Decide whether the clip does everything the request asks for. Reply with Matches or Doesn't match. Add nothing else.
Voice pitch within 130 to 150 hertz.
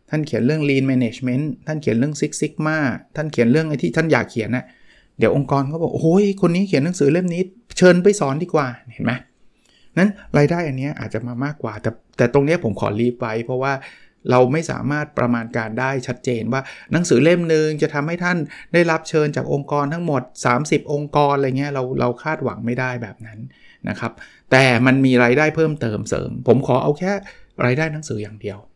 Matches